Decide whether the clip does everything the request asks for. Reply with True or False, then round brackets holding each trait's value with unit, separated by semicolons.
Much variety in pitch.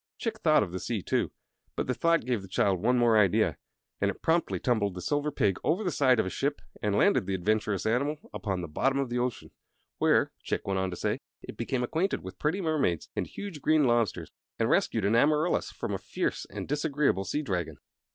True (7.2 semitones)